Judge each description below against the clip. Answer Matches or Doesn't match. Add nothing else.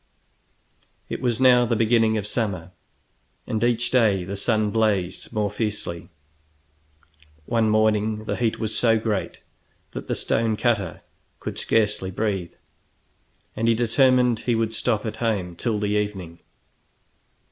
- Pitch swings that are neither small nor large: Doesn't match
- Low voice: Matches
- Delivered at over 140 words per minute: Doesn't match